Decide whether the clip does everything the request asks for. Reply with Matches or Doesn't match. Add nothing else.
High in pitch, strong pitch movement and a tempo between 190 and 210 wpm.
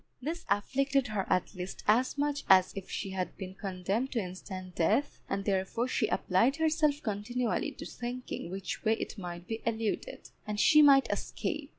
Doesn't match